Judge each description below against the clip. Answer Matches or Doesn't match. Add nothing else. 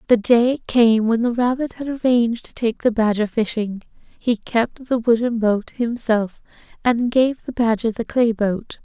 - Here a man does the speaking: Doesn't match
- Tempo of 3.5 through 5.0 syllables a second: Matches